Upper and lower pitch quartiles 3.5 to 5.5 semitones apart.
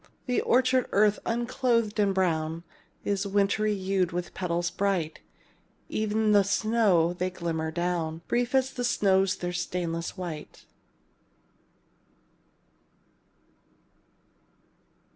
Yes: average, 3.8 semitones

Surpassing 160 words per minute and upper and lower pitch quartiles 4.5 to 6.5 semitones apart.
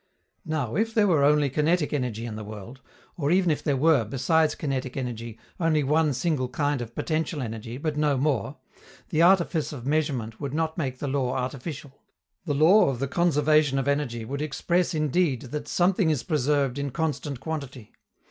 No: average, 180 wpm; average, 3.5 semitones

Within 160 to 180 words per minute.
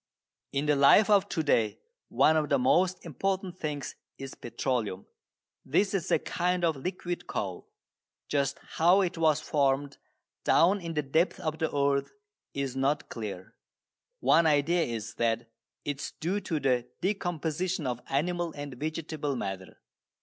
No: average, 150 wpm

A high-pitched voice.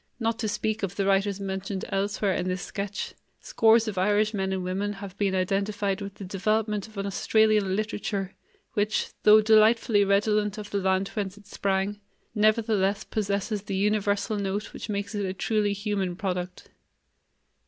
Yes: high, 200 Hz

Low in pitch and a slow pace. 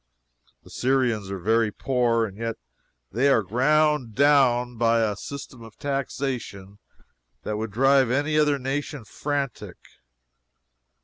Yes: low, 125 Hz; slow, 125 wpm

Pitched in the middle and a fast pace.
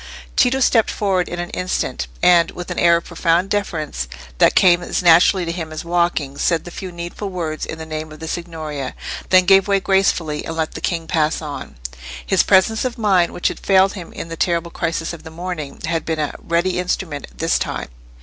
Yes: medium, 170 Hz; fast, 210 wpm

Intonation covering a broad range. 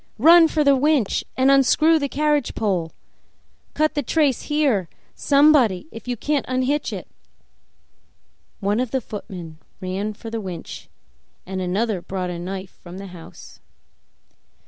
Yes: wide, 7.5 semitones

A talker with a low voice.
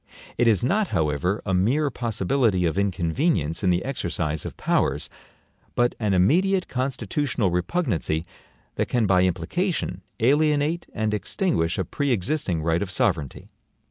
Yes: low, 105 Hz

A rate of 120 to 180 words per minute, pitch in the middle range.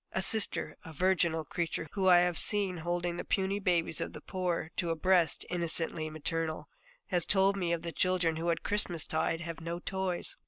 No: average, 190 wpm; medium, 175 Hz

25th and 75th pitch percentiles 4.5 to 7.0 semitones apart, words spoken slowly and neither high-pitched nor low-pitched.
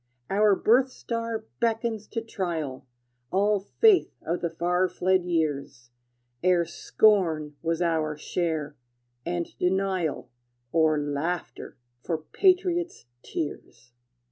Yes: average, 5.1 semitones; slow, 105 wpm; medium, 175 Hz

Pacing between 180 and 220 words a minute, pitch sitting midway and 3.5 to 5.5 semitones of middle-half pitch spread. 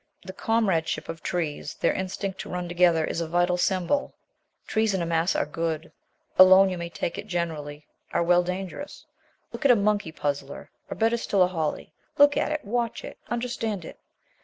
Yes: average, 185 wpm; medium, 180 Hz; average, 4.0 semitones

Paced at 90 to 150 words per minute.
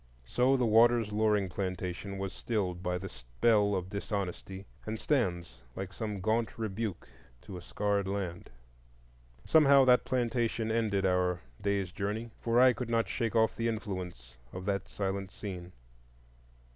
Yes: average, 145 wpm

